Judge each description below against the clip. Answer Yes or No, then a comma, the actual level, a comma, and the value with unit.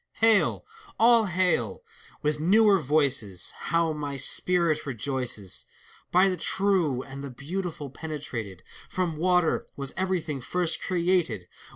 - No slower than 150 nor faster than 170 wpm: No, average, 140 wpm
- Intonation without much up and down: No, average, 5.1 semitones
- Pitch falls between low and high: Yes, medium, 160 Hz